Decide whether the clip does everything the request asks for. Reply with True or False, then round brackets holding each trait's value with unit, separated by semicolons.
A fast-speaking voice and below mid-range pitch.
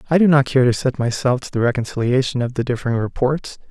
True (225 wpm; 130 Hz)